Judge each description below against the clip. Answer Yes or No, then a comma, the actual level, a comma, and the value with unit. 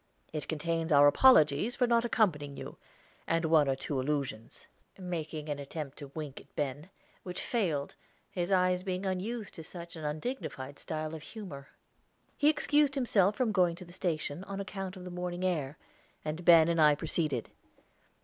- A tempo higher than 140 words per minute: Yes, average, 170 wpm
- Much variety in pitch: No, average, 4.1 semitones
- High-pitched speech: No, medium, 170 Hz